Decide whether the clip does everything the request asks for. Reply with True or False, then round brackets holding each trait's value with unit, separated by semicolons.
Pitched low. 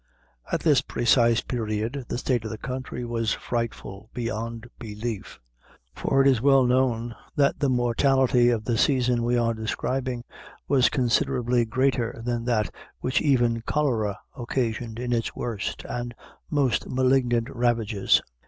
True (120 Hz)